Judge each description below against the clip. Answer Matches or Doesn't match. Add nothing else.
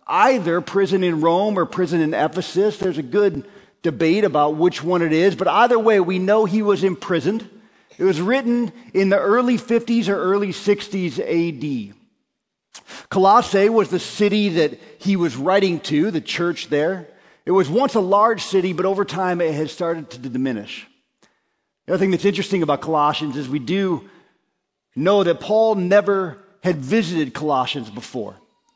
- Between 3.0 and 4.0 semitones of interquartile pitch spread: Matches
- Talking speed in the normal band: Matches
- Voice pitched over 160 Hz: Matches